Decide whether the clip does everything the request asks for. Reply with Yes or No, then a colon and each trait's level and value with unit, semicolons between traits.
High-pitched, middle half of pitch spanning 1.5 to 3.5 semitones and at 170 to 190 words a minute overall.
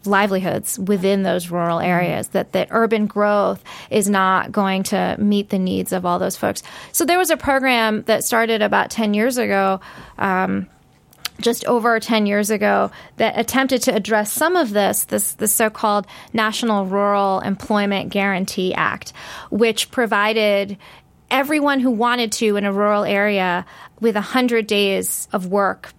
No: high, 205 Hz; narrow, 2.6 semitones; average, 155 wpm